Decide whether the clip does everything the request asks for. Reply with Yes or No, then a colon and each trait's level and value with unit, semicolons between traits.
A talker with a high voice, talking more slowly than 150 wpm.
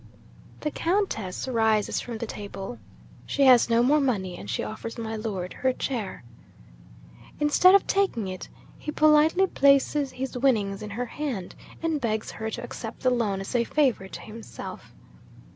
No: high, 235 Hz; average, 160 wpm